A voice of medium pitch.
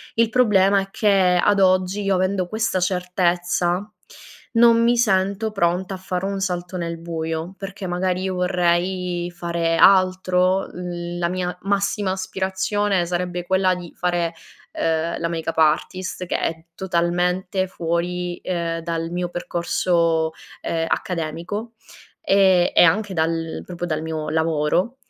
Yes: medium, 180 Hz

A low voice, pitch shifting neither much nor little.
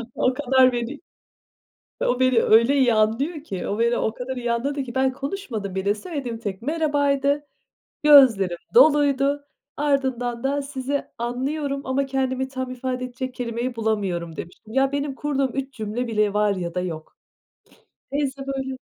No: very high, 260 Hz; average, 3.3 semitones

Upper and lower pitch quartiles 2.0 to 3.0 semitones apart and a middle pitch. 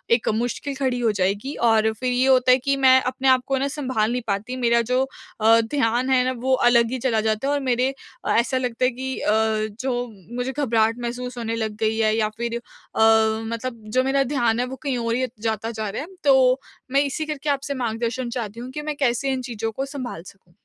No: average, 2.7 semitones; high, 245 Hz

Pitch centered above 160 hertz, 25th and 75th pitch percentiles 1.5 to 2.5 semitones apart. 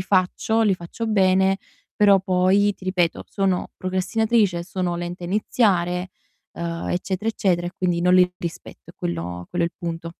Yes: medium, 185 Hz; narrow, 2.1 semitones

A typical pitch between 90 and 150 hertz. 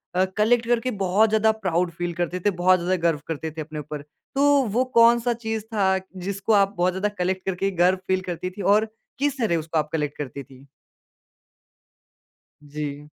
No: medium, 185 Hz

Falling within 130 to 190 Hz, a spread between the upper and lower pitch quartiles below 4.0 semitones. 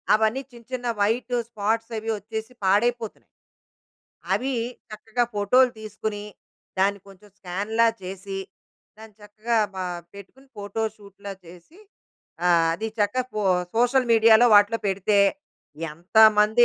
No: high, 215 Hz; narrow, 2.4 semitones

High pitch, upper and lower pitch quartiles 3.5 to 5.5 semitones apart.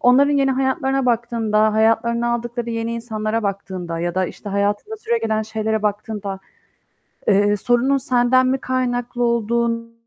No: high, 230 Hz; narrow, 2.4 semitones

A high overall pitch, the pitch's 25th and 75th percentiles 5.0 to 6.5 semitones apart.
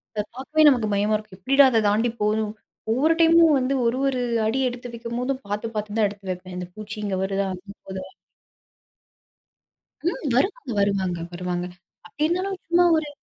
Yes: high, 220 Hz; wide, 5.4 semitones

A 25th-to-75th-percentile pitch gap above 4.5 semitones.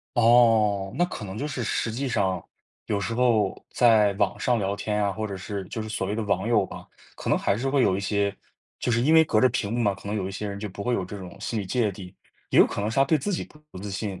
No: average, 3.3 semitones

